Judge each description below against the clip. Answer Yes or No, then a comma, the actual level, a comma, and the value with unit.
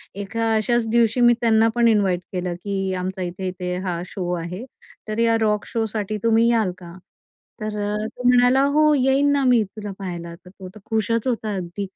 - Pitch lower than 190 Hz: No, high, 215 Hz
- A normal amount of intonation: Yes, average, 3.8 semitones